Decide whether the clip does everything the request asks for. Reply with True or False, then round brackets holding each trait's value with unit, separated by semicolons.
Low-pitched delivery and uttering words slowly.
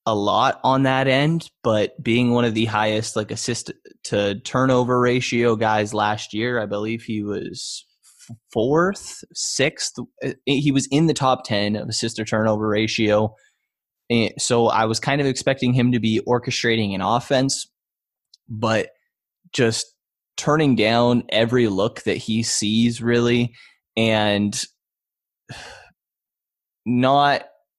True (115 Hz; 130 wpm)